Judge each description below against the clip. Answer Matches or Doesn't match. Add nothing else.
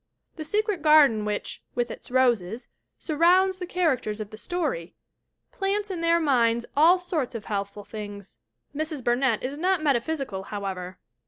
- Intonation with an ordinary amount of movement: Doesn't match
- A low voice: Doesn't match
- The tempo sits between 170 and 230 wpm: Doesn't match